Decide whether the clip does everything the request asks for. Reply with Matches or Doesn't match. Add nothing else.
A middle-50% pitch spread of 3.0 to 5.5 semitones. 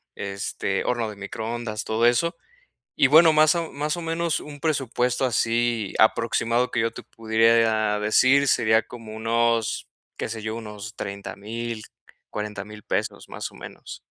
Doesn't match